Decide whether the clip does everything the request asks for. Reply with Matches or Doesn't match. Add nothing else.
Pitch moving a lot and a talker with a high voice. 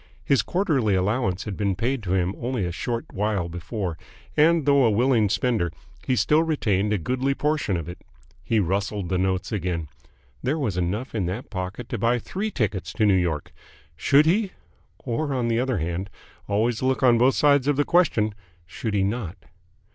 Doesn't match